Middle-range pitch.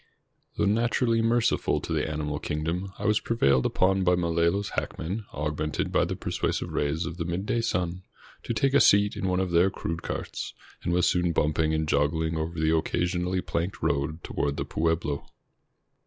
No: very low, 85 Hz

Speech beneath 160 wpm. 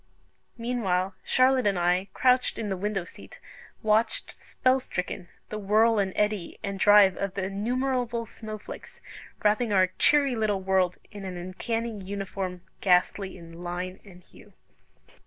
Yes: average, 145 wpm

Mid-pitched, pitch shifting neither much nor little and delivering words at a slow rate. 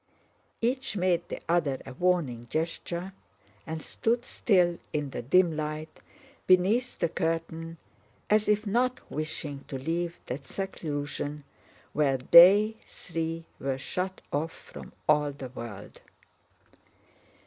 Yes: medium, 165 Hz; average, 4.2 semitones; slow, 120 wpm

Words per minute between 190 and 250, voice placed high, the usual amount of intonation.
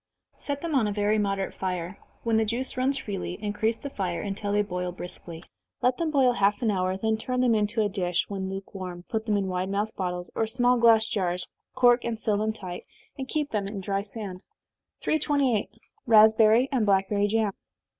Yes: average, 195 wpm; high, 210 Hz; average, 3.2 semitones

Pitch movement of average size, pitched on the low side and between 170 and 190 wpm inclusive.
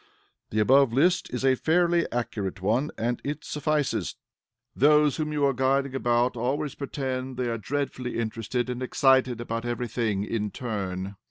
No: average, 3.4 semitones; low, 130 Hz; average, 160 wpm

